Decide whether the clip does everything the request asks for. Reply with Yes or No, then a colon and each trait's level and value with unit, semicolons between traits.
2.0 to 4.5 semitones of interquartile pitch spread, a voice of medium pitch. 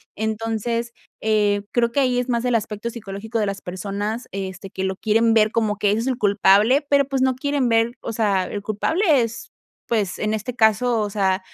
No: narrow, 2.6 semitones; high, 220 Hz